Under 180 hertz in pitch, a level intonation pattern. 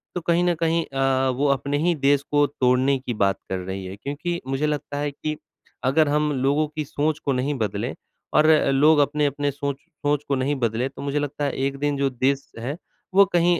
Yes: medium, 140 Hz; narrow, 2.1 semitones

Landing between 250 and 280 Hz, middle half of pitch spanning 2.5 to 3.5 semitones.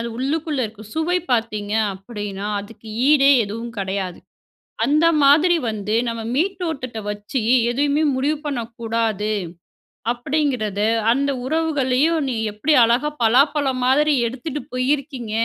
No: very high, 255 Hz; average, 5.1 semitones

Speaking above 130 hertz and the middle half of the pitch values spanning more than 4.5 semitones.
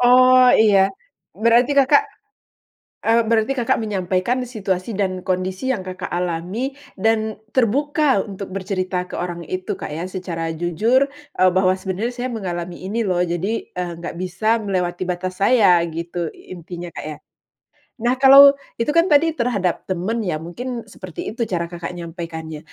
Yes: high, 190 Hz; average, 5.0 semitones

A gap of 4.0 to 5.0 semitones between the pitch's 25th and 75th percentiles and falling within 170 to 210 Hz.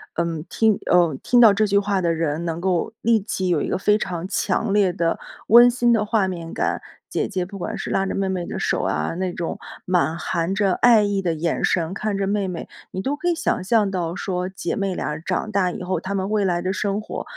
No: average, 3.1 semitones; high, 190 Hz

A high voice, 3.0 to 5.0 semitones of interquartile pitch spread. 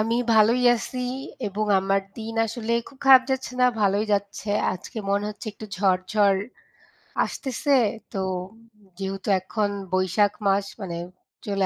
No: high, 205 Hz; narrow, 2.5 semitones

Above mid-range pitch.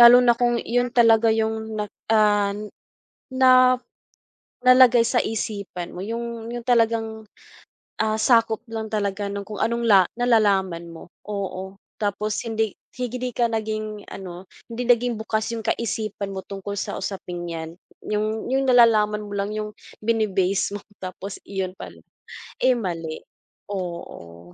Yes: high, 215 Hz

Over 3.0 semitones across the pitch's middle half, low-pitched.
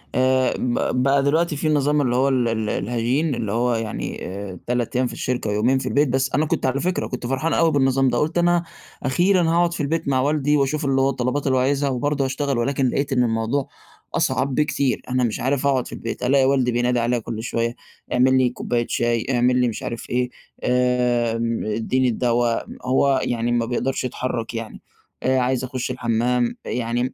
No: narrow, 2.4 semitones; low, 125 Hz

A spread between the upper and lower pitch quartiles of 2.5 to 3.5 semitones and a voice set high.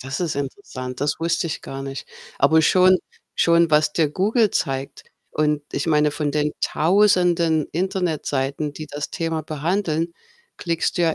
No: average, 2.8 semitones; medium, 155 Hz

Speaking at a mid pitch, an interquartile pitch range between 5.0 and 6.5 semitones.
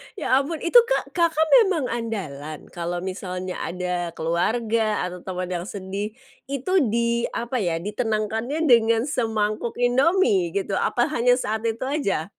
No: high, 220 Hz; average, 5.3 semitones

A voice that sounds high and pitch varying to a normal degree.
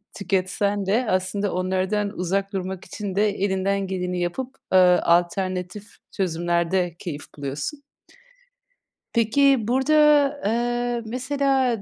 Yes: high, 195 Hz; average, 4.2 semitones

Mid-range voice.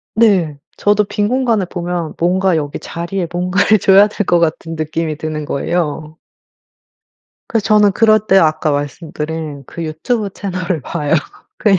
Yes: medium, 175 Hz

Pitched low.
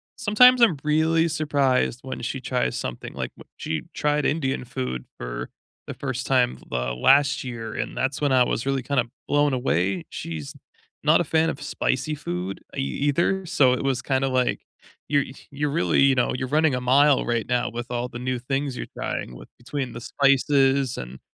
Yes: low, 130 Hz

